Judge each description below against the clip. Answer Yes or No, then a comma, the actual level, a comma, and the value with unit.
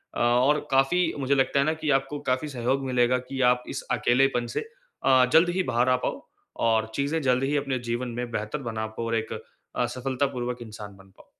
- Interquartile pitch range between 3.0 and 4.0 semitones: No, narrow, 2.4 semitones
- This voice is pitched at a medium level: No, low, 130 Hz